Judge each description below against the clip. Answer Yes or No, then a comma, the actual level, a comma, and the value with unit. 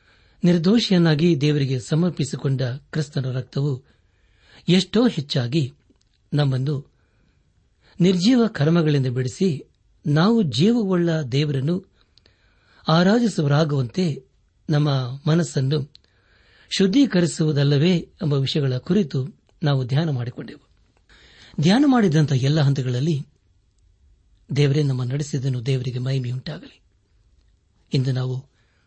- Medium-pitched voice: Yes, medium, 145 Hz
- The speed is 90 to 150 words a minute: No, average, 70 wpm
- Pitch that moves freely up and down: No, average, 4.7 semitones